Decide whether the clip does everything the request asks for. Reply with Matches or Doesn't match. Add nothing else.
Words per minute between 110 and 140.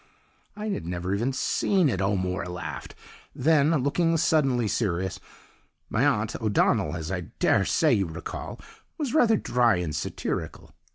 Matches